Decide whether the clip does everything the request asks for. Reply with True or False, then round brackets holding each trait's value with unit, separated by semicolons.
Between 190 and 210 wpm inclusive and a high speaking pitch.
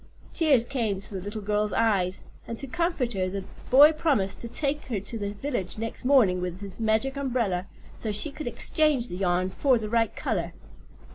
True (195 wpm; 225 Hz)